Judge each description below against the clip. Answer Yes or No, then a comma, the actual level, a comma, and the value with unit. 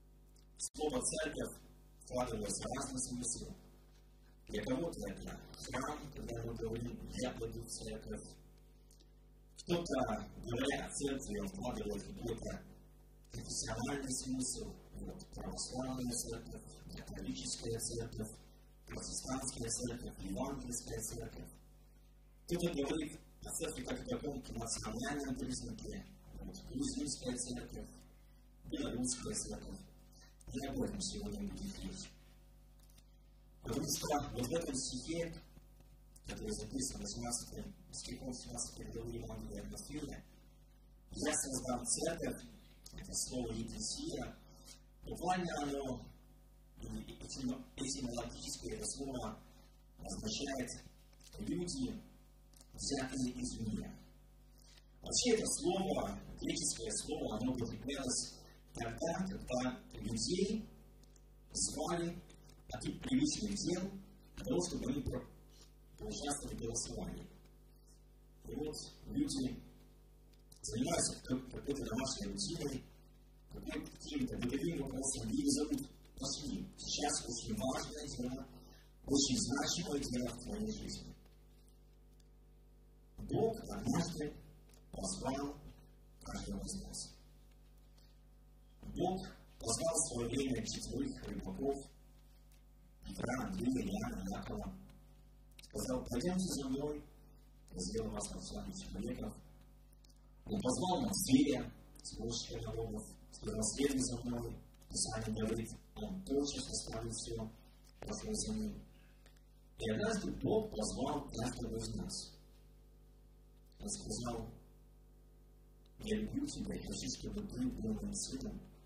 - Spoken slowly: Yes, slow, 95 wpm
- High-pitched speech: No, low, 130 Hz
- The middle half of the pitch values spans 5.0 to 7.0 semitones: No, average, 4.3 semitones